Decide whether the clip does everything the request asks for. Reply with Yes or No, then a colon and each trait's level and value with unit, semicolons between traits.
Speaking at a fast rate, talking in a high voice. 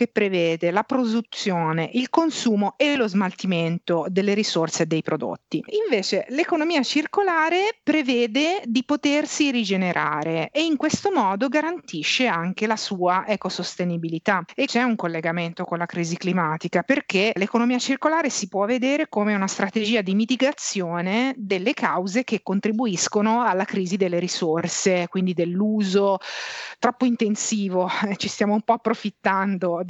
No: average, 135 wpm; high, 210 Hz